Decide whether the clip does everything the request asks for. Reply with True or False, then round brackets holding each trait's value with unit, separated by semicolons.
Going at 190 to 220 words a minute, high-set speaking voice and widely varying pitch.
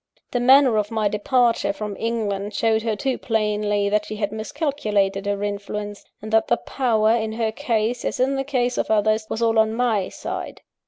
False (200 wpm; 220 Hz; 2.4 semitones)